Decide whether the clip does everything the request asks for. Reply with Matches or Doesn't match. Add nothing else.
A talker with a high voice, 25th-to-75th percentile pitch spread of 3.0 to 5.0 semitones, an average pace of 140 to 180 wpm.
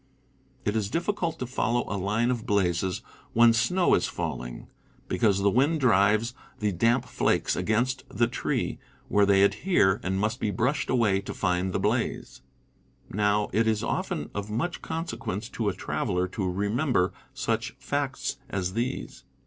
Doesn't match